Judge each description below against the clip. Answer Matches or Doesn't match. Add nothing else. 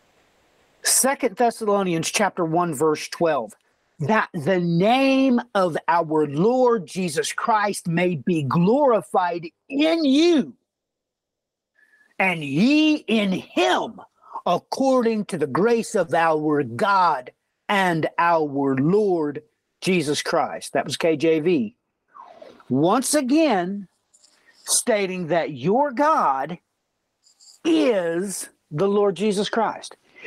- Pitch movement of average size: Doesn't match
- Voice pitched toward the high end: Matches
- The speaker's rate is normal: Doesn't match